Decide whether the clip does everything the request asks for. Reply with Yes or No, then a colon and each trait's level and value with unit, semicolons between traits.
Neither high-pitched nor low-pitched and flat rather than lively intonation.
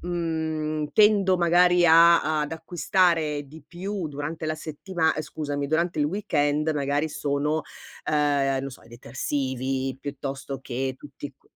No: medium, 155 Hz; average, 3.0 semitones